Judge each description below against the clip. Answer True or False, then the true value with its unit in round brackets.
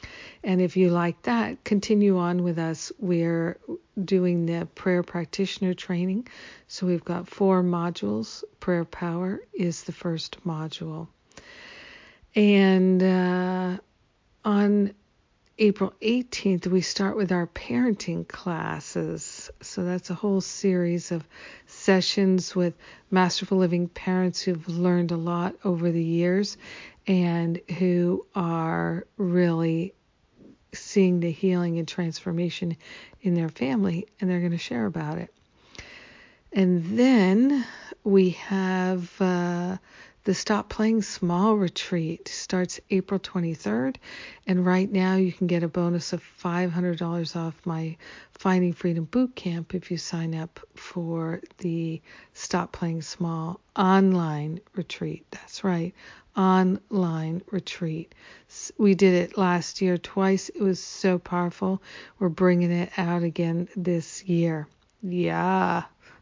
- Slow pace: True (125 wpm)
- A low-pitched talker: False (180 Hz)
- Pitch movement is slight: True (2.0 semitones)